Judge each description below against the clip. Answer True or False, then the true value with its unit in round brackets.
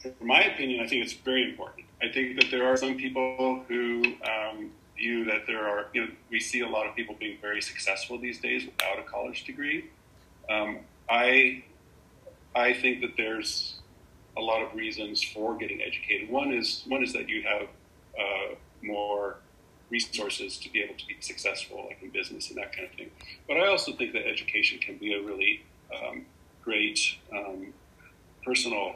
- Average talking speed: True (185 wpm)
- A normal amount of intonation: True (3.3 semitones)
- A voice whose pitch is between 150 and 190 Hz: False (120 Hz)